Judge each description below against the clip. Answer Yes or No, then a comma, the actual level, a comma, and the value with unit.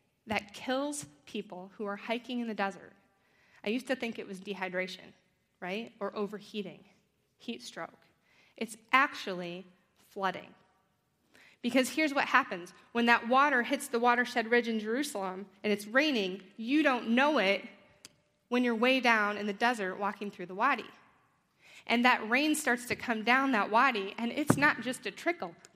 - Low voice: No, high, 220 Hz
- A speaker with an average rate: Yes, average, 165 wpm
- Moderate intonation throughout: Yes, average, 4.0 semitones